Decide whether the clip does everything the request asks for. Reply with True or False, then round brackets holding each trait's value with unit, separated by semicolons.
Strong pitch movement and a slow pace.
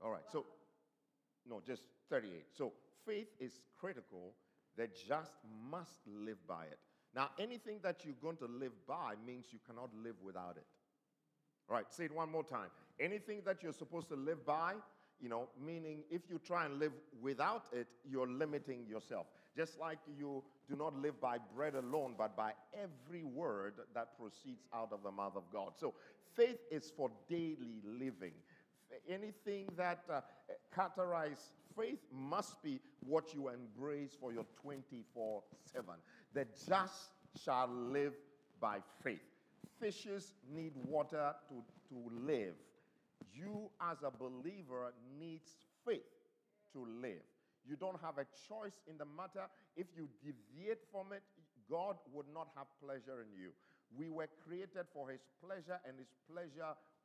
False (6.0 semitones; 155 wpm)